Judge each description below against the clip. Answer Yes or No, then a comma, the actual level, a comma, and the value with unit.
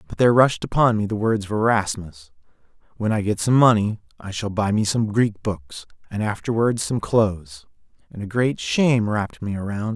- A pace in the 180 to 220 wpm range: Yes, average, 195 wpm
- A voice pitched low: Yes, low, 110 Hz